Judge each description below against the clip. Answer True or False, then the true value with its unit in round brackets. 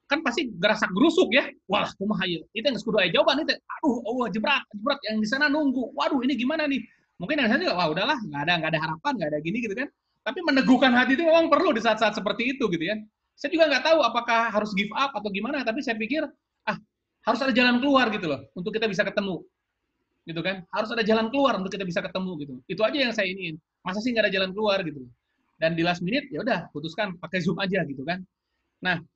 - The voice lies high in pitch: True (220 Hz)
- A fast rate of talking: True (235 wpm)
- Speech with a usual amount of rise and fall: False (6.4 semitones)